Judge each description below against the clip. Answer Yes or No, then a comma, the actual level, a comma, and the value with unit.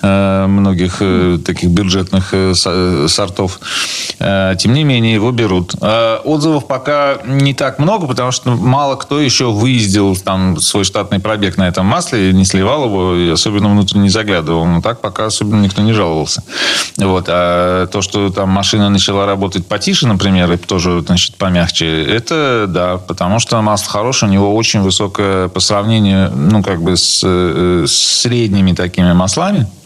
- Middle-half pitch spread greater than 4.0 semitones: No, average, 3.1 semitones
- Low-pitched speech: Yes, low, 100 Hz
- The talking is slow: No, average, 155 wpm